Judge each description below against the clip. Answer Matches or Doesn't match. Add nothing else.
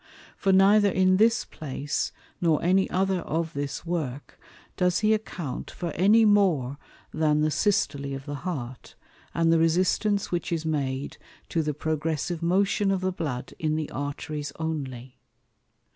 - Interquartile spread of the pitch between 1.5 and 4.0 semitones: Doesn't match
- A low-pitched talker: Doesn't match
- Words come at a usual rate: Matches